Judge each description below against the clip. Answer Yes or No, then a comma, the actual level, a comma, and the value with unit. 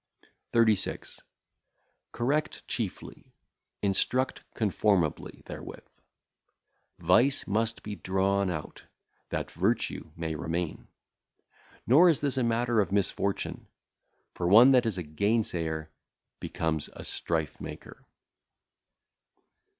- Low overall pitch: Yes, low, 100 Hz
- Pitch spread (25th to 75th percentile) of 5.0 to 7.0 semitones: Yes, wide, 5.5 semitones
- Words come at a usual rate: No, slow, 95 wpm